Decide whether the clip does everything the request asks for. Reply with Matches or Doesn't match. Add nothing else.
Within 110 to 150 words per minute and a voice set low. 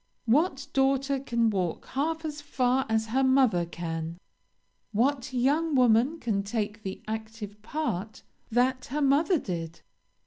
Doesn't match